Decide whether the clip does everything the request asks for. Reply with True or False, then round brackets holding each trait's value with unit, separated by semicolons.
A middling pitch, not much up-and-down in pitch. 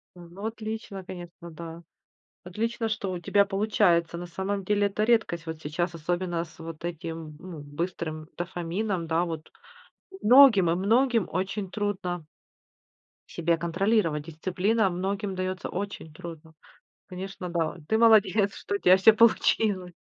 False (180 Hz; 3.3 semitones)